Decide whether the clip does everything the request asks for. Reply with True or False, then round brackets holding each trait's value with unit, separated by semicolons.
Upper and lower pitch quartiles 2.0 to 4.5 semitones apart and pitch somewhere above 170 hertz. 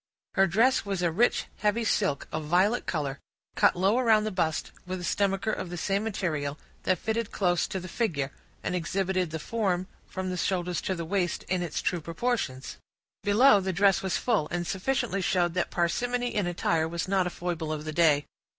True (3.2 semitones; 185 Hz)